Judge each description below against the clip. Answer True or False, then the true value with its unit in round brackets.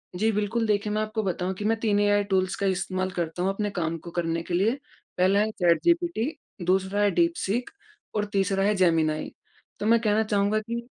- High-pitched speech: True (205 Hz)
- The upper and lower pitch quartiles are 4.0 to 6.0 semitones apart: False (2.7 semitones)